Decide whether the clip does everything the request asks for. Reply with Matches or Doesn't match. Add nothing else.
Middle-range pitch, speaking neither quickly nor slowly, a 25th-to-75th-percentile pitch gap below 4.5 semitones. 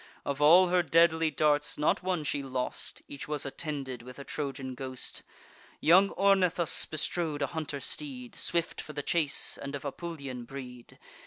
Matches